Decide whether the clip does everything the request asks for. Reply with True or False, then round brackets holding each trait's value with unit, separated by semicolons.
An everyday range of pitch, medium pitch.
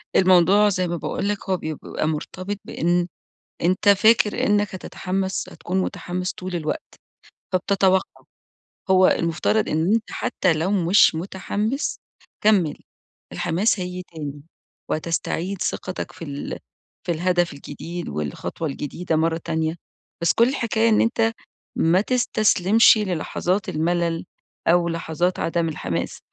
True (3.3 semitones; 180 Hz)